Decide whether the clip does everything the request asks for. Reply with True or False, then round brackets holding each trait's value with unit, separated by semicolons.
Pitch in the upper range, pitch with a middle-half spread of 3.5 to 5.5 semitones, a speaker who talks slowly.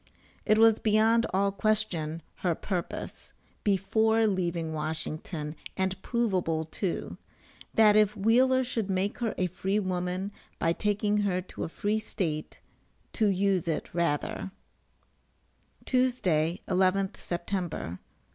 True (195 Hz; 3.8 semitones; 120 wpm)